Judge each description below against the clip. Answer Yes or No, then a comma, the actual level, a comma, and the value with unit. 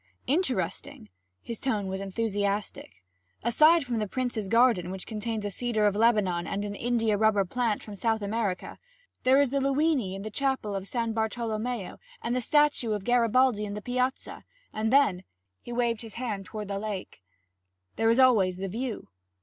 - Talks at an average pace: Yes, average, 175 wpm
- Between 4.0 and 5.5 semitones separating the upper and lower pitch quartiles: No, average, 3.5 semitones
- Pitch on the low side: No, high, 220 Hz